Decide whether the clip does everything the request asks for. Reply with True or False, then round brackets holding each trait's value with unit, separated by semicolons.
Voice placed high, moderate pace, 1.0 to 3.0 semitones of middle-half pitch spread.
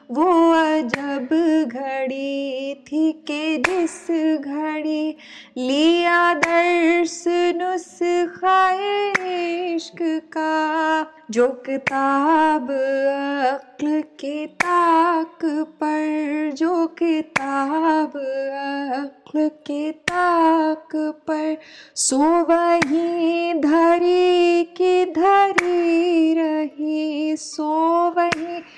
False (315 Hz; 65 wpm; 2.4 semitones)